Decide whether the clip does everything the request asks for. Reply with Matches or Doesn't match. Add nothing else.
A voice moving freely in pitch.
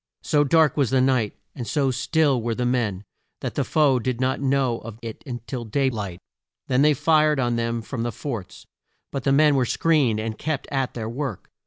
Doesn't match